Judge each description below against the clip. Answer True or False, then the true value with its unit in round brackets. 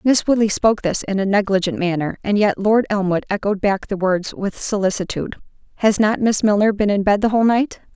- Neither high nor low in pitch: False (205 Hz)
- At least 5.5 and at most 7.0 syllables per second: True (5.7 syllables/s)